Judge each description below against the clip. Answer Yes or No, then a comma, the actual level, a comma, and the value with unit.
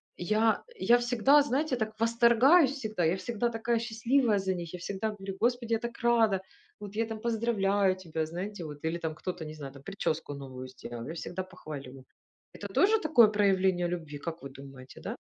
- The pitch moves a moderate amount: No, wide, 6.1 semitones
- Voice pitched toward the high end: Yes, high, 200 Hz